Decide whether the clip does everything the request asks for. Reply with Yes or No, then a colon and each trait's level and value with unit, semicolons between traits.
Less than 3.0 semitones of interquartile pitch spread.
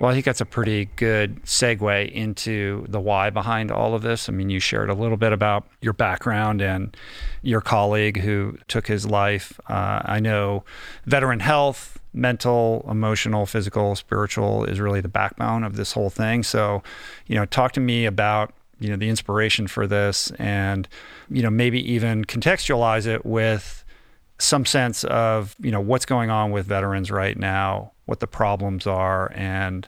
Yes: narrow, 2.5 semitones